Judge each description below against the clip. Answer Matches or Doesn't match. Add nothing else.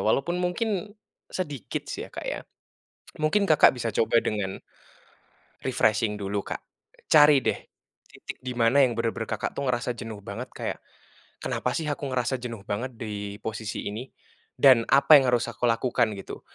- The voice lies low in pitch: Matches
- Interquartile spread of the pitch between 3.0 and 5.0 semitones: Matches